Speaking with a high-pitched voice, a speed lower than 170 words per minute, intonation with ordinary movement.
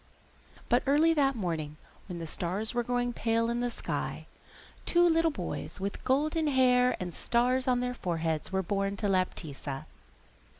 No: high, 235 Hz; average, 160 wpm; wide, 6.0 semitones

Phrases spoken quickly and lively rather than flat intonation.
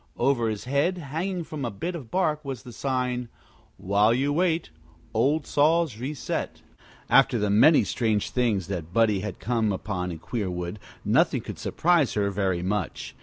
No: average, 165 wpm; wide, 6.1 semitones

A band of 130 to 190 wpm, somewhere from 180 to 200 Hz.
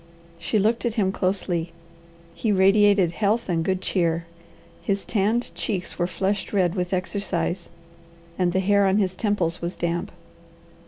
Yes: average, 150 wpm; high, 190 Hz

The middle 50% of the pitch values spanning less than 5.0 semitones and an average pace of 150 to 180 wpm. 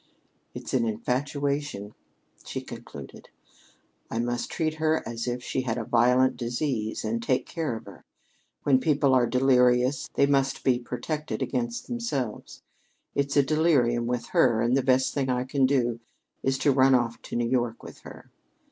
Yes: average, 2.8 semitones; average, 165 wpm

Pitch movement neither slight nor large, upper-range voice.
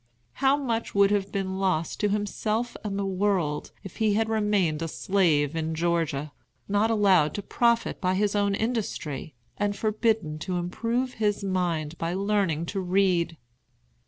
Yes: average, 3.8 semitones; high, 195 Hz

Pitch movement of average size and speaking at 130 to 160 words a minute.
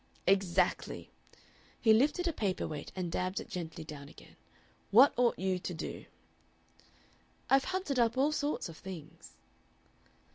No: wide, 7.8 semitones; average, 140 wpm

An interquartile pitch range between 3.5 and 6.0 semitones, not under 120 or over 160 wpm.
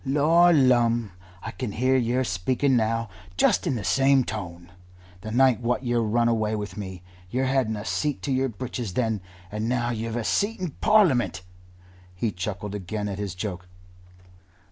No: average, 4.0 semitones; average, 170 wpm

